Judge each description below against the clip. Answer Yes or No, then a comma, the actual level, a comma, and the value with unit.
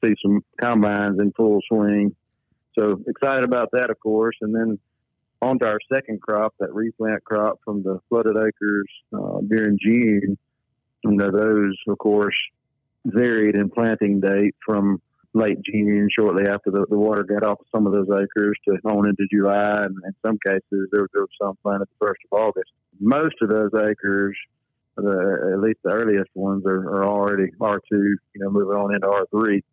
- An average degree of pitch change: No, narrow, 1.5 semitones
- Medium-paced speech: Yes, average, 180 wpm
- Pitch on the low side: Yes, low, 105 Hz